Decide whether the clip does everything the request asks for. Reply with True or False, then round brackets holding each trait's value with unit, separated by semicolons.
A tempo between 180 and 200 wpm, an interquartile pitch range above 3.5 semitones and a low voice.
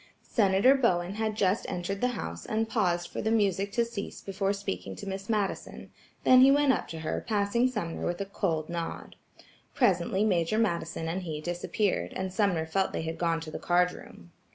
False (195 wpm; 4.1 semitones; 195 Hz)